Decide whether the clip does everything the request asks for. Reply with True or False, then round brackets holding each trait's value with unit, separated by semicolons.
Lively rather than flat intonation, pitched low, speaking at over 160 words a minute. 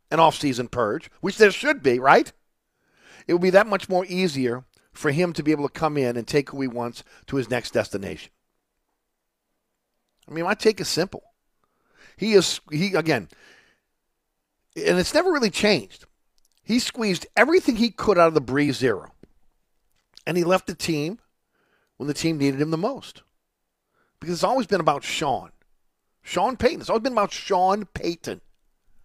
False (6.3 semitones; 175 Hz; 175 wpm)